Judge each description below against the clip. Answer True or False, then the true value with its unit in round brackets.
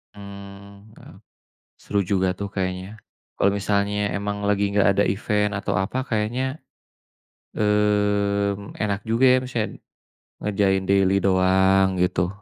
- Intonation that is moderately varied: False (1.2 semitones)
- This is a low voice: True (100 Hz)